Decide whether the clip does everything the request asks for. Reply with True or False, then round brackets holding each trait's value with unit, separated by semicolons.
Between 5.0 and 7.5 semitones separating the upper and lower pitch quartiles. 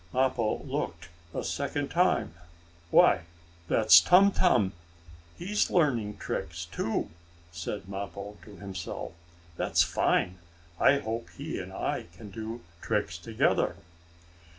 False (4.1 semitones)